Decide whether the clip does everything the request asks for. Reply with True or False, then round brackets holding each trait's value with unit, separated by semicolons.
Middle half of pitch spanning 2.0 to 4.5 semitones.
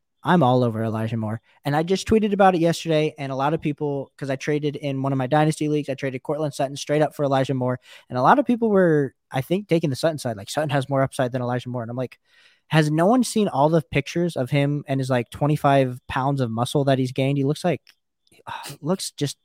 True (2.9 semitones)